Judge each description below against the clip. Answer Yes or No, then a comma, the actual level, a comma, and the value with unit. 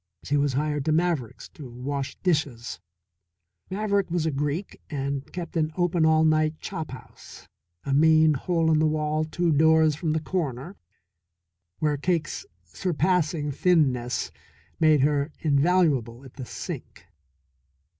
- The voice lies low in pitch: No, medium, 155 Hz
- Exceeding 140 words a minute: No, slow, 135 wpm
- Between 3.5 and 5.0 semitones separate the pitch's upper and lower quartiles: No, average, 2.7 semitones